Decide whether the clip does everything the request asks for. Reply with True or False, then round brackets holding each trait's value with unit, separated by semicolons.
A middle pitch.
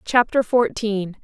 False (220 Hz)